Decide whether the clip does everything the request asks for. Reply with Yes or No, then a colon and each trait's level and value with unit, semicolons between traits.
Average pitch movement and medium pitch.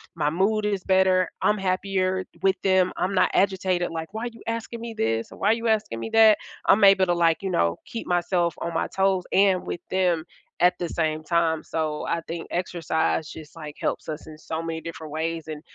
Yes: average, 3.2 semitones; medium, 180 Hz